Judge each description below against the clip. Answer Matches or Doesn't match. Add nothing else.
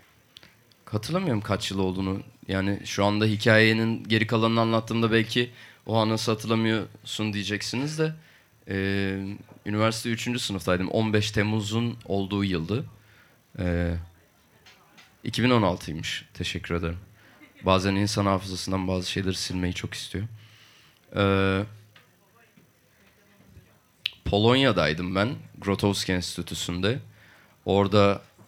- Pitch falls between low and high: Doesn't match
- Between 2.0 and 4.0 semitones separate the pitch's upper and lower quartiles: Matches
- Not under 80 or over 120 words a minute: Matches